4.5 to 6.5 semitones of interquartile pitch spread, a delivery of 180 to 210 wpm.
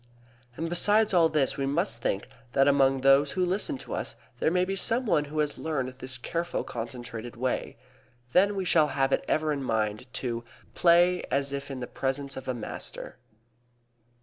Yes: average, 4.9 semitones; average, 185 wpm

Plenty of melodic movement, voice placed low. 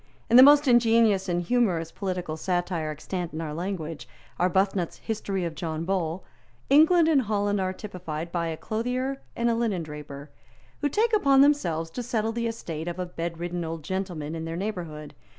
No: wide, 5.8 semitones; medium, 185 Hz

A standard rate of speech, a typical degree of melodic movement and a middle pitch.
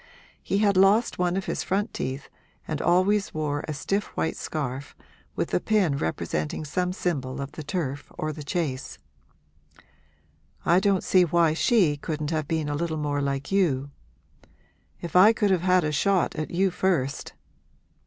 Yes: average, 165 wpm; average, 4.6 semitones; medium, 160 Hz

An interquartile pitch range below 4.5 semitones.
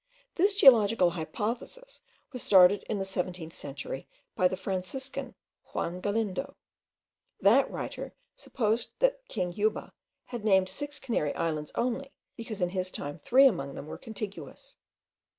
No: wide, 5.6 semitones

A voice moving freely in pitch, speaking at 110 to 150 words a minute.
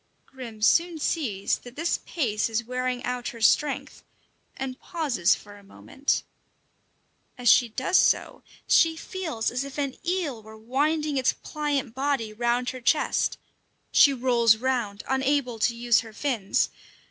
No: average, 3.9 semitones; average, 145 wpm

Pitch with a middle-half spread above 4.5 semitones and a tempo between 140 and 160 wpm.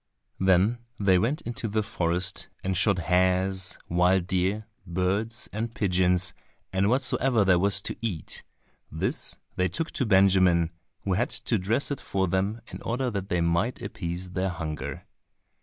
No: average, 3.1 semitones; average, 155 wpm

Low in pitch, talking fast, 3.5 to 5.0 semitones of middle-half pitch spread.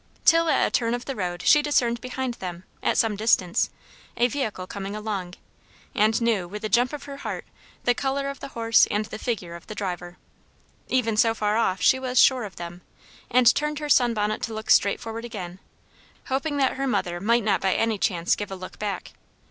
No: high, 225 Hz; fast, 210 wpm; average, 4.4 semitones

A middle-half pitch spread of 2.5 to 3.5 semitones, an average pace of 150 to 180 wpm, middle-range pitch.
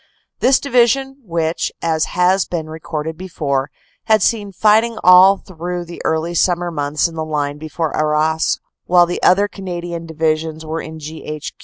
Yes: average, 2.9 semitones; average, 160 wpm; medium, 165 Hz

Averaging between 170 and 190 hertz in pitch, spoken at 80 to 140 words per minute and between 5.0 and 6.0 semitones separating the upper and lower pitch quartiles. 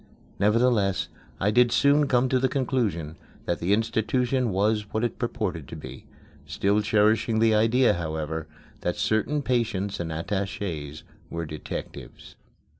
No: low, 105 Hz; slow, 135 wpm; wide, 5.6 semitones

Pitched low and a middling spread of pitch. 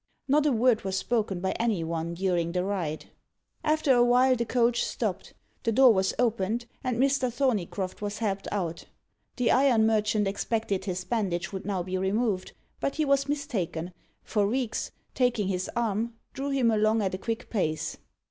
No: high, 215 Hz; average, 4.5 semitones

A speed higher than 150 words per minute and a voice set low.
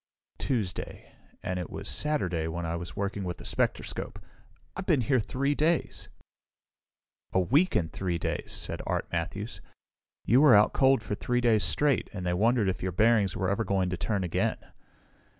Yes: average, 175 wpm; low, 100 Hz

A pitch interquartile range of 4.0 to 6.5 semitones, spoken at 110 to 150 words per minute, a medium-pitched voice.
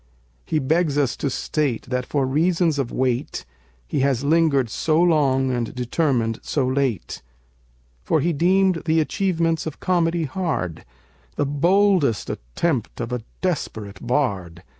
Yes: average, 4.9 semitones; average, 140 wpm; medium, 145 Hz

